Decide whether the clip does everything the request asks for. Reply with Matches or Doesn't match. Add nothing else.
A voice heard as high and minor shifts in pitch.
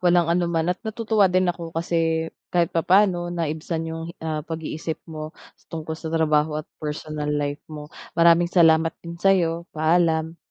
Doesn't match